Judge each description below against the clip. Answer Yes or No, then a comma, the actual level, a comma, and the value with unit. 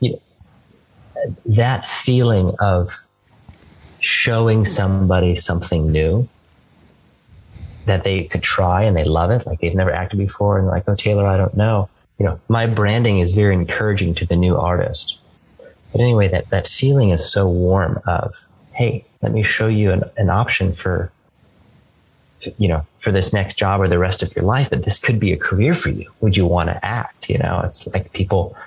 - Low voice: Yes, very low, 95 Hz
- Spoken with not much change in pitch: No, average, 3.1 semitones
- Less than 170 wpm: No, average, 185 wpm